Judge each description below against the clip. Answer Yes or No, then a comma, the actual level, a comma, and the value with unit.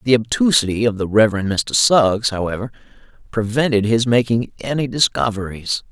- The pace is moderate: No, slow, 130 wpm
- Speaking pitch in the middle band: No, low, 115 Hz